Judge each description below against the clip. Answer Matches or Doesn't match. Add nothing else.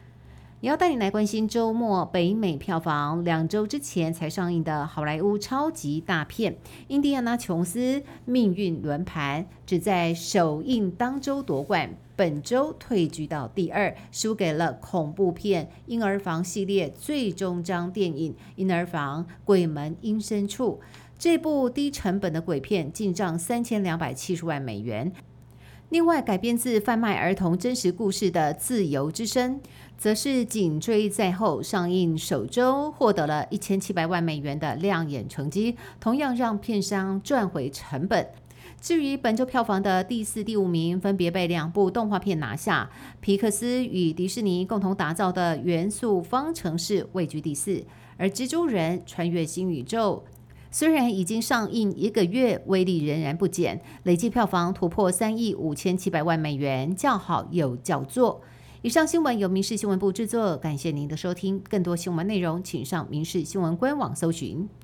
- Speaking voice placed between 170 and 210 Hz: Matches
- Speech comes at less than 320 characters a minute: Matches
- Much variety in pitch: Doesn't match